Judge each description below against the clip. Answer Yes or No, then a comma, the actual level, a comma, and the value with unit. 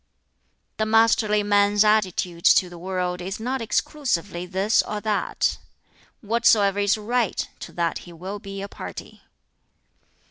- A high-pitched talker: Yes, high, 205 Hz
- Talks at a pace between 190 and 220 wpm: No, slow, 135 wpm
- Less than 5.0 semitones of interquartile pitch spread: Yes, average, 2.9 semitones